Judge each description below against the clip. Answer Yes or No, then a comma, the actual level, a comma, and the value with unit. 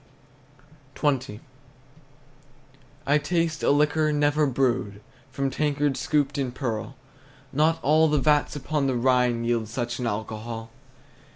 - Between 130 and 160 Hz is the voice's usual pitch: Yes, low, 135 Hz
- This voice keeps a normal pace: No, slow, 120 wpm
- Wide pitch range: No, average, 3.7 semitones